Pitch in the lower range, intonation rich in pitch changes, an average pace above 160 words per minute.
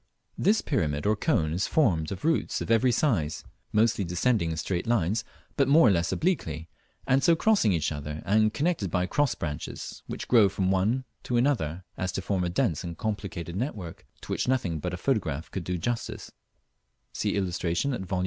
Yes: low, 100 Hz; wide, 6.6 semitones; average, 190 wpm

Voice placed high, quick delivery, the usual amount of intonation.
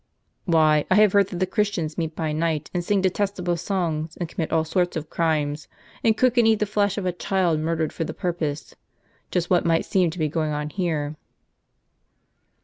No: medium, 170 Hz; fast, 215 wpm; average, 3.4 semitones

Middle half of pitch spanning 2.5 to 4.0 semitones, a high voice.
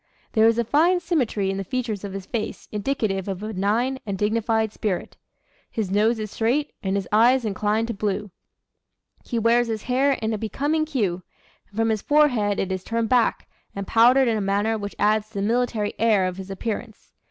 Yes: average, 2.9 semitones; high, 220 Hz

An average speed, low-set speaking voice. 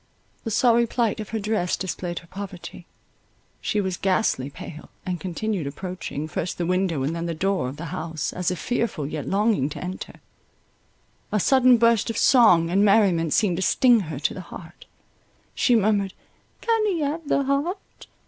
No: average, 175 wpm; high, 190 Hz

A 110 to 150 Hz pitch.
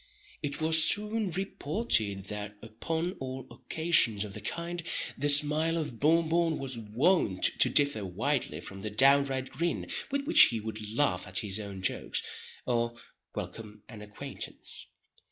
Yes: low, 135 Hz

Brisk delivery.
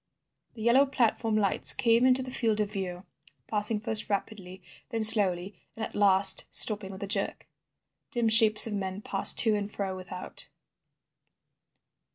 No: average, 155 wpm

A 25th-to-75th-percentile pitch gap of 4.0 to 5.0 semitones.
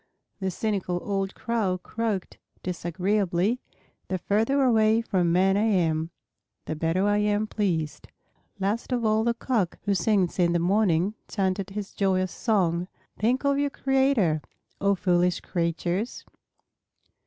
No: average, 3.6 semitones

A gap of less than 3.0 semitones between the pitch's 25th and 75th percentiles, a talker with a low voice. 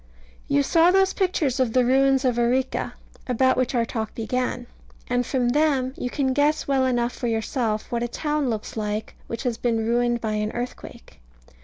No: narrow, 2.5 semitones; high, 245 Hz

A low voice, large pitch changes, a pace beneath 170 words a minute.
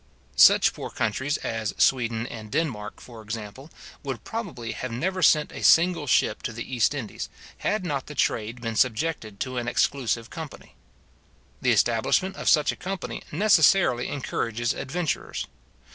Yes: low, 130 Hz; wide, 5.8 semitones; average, 150 wpm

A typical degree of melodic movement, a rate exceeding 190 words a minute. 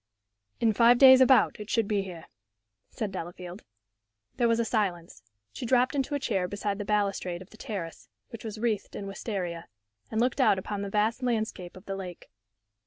No: average, 3.7 semitones; average, 185 wpm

